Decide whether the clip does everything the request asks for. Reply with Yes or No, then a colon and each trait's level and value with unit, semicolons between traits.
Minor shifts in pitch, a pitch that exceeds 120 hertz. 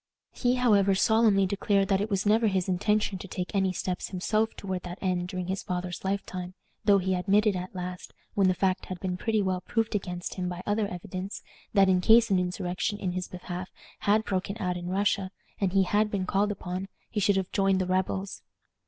Yes: narrow, 2.0 semitones; high, 190 Hz